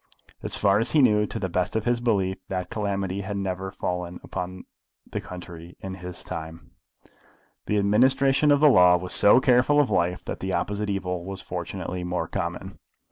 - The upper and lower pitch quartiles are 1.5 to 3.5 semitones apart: Yes, average, 2.8 semitones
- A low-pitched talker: Yes, very low, 95 Hz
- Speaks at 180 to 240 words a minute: Yes, average, 185 wpm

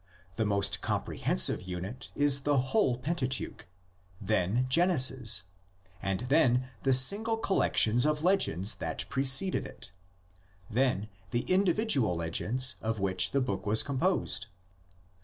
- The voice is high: No, low, 130 Hz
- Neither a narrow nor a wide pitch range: No, wide, 5.7 semitones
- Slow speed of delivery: Yes, slow, 120 wpm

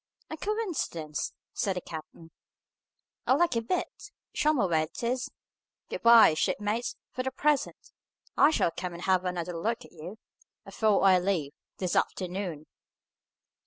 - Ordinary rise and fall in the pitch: No, wide, 6.3 semitones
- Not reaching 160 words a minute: Yes, average, 145 wpm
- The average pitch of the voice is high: Yes, high, 195 Hz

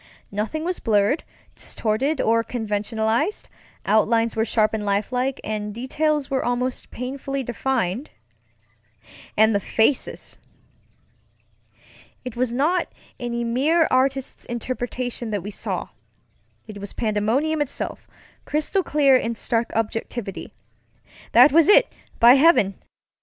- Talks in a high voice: Yes, high, 240 Hz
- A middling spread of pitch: Yes, average, 3.9 semitones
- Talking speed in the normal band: No, slow, 115 wpm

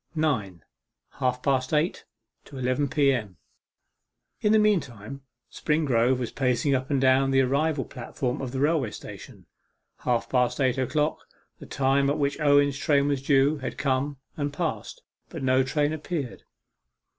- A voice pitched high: No, low, 135 Hz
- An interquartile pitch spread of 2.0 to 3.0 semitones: Yes, narrow, 2.4 semitones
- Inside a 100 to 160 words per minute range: Yes, average, 150 wpm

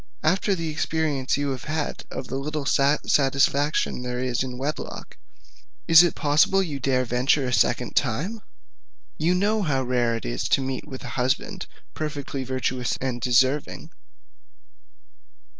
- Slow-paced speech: No, average, 145 wpm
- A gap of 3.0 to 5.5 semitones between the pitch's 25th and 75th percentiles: Yes, average, 3.3 semitones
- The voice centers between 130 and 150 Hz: Yes, low, 135 Hz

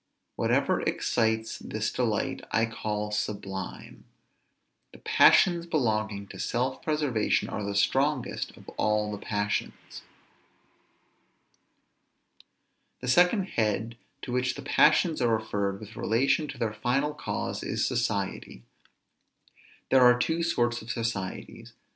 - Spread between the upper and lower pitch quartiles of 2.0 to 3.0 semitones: No, average, 4.1 semitones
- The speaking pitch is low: Yes, low, 115 Hz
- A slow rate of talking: Yes, slow, 115 wpm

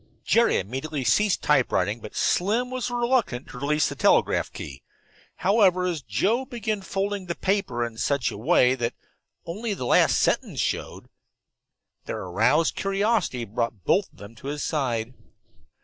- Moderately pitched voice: Yes, medium, 160 Hz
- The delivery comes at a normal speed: Yes, average, 150 wpm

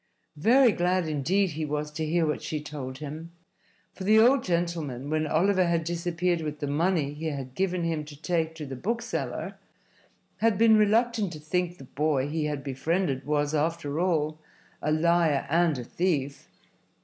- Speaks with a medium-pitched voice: Yes, medium, 160 Hz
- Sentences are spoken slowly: No, average, 175 wpm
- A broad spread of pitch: No, average, 3.3 semitones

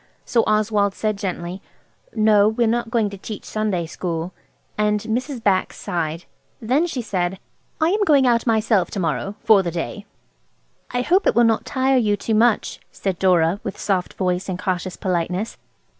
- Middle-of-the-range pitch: No, high, 210 Hz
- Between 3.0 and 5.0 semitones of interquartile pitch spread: Yes, average, 3.8 semitones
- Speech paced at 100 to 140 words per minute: No, average, 170 wpm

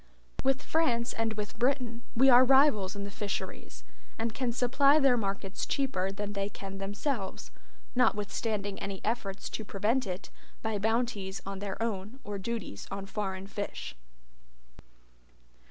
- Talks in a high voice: Yes, high, 210 Hz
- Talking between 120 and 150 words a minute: Yes, average, 140 wpm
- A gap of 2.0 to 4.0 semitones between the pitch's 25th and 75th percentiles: Yes, average, 3.7 semitones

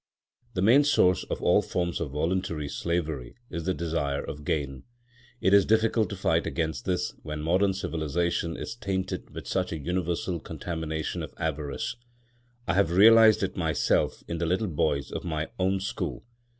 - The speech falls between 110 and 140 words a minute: No, average, 165 wpm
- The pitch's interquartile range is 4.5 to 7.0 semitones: No, average, 3.3 semitones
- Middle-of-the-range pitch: No, very low, 85 Hz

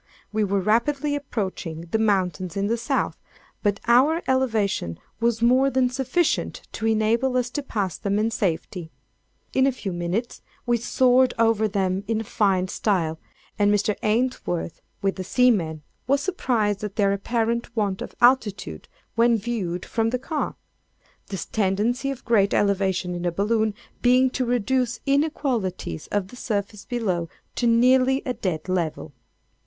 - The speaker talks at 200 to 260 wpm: No, average, 150 wpm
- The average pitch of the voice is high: Yes, high, 220 Hz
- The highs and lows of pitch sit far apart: No, average, 4.3 semitones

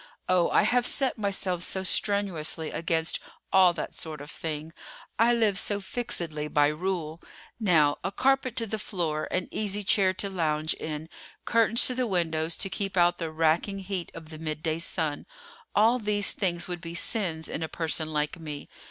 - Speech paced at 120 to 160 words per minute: No, average, 175 wpm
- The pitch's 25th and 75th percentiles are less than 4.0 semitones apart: No, average, 4.3 semitones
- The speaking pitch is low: No, medium, 175 Hz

